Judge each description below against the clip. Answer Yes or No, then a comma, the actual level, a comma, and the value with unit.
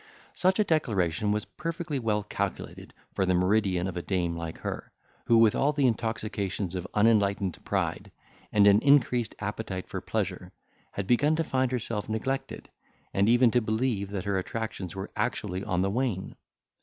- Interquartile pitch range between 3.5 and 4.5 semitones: Yes, average, 4.2 semitones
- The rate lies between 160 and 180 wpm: Yes, average, 170 wpm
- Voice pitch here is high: No, low, 105 Hz